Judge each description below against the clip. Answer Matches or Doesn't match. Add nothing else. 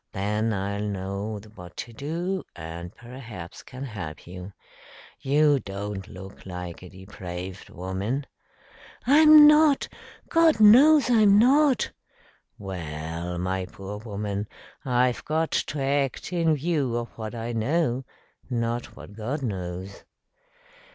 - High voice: Doesn't match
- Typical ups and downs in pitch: Doesn't match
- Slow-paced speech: Matches